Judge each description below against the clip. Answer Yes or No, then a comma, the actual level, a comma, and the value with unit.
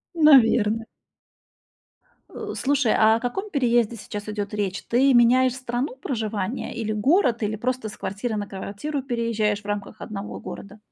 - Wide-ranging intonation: No, average, 3.4 semitones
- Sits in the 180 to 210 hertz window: No, high, 225 Hz